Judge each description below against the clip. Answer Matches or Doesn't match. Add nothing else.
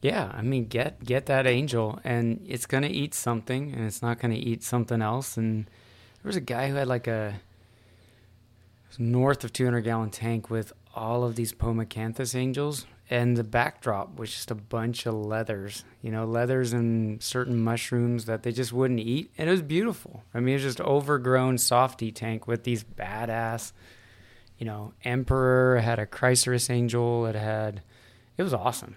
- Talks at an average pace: Matches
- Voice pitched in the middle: Doesn't match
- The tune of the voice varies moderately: Doesn't match